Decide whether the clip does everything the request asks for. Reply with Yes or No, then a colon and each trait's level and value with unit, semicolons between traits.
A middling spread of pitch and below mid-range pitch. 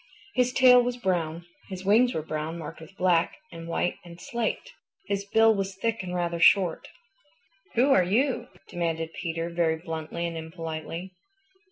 No: average, 4.9 semitones; medium, 175 Hz